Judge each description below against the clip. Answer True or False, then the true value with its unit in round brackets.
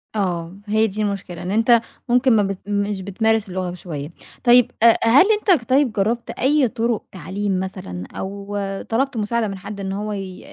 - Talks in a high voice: True (205 Hz)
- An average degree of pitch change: True (3.5 semitones)